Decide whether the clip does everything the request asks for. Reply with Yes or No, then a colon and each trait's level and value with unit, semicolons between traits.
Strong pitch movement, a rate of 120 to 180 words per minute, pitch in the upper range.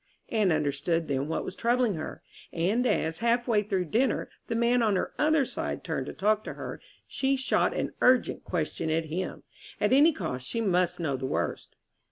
No: wide, 6.7 semitones; average, 195 wpm; high, 200 Hz